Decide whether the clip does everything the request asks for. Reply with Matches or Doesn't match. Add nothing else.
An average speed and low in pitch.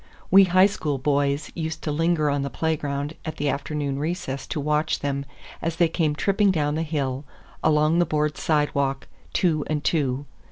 Doesn't match